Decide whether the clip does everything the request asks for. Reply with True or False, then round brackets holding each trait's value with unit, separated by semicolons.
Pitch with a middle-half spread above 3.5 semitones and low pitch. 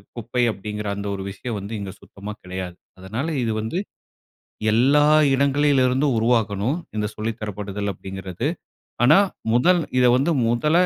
True (4.7 semitones; 115 Hz)